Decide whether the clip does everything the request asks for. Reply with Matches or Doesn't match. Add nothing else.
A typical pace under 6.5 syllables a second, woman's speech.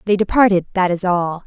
Matches